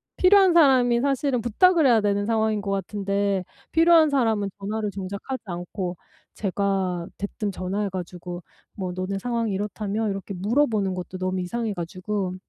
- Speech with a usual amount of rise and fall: Yes, average, 3.9 semitones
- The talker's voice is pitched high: Yes, high, 205 Hz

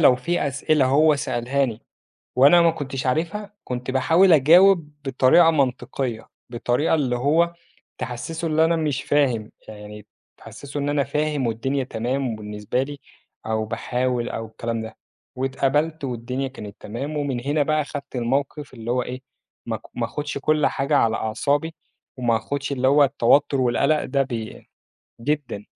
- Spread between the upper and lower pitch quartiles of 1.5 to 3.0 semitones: No, average, 3.6 semitones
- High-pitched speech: No, low, 135 Hz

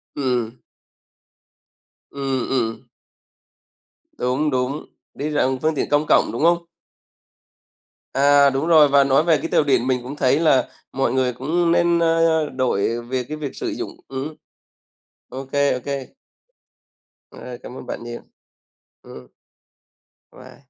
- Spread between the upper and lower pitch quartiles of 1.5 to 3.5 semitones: Yes, average, 3.1 semitones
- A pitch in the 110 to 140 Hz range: Yes, low, 135 Hz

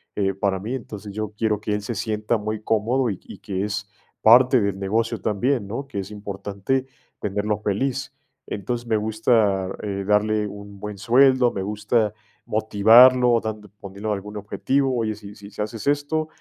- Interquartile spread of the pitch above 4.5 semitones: No, narrow, 2.6 semitones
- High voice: No, low, 105 Hz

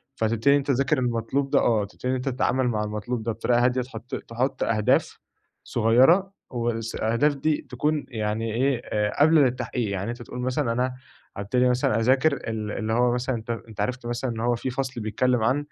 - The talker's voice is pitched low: Yes, low, 125 Hz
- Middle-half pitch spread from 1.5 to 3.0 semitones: Yes, narrow, 2.6 semitones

